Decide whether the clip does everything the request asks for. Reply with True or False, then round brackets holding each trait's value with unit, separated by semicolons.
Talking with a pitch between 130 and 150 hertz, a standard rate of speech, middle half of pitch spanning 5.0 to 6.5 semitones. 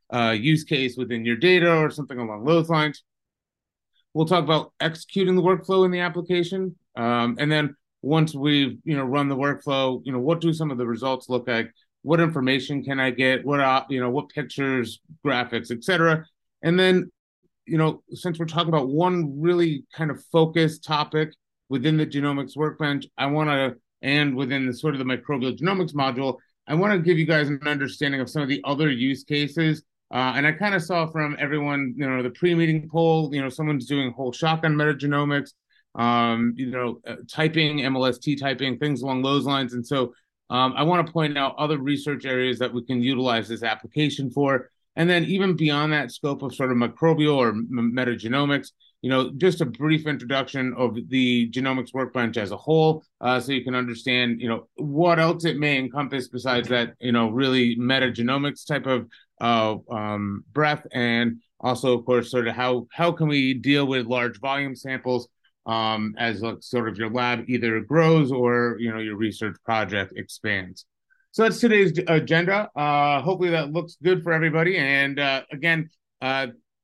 False (140 Hz; 190 wpm; 3.9 semitones)